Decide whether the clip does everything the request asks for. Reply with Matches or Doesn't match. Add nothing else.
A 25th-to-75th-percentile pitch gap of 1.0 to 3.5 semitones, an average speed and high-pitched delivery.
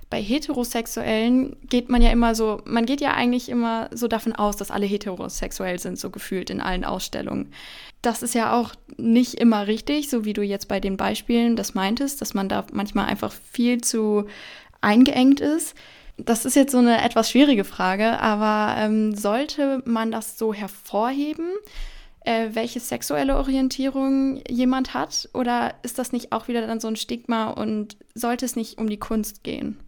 Matches